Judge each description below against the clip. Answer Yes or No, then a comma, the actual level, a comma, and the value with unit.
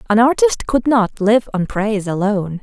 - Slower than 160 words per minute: No, average, 185 wpm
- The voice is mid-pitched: No, high, 220 Hz